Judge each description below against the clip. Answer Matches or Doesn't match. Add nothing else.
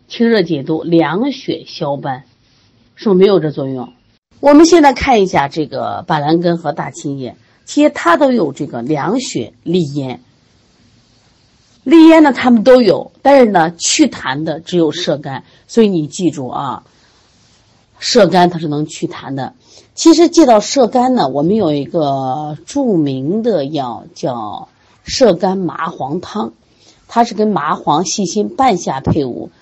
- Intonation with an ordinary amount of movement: Doesn't match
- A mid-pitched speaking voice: Matches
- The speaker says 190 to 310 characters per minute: Matches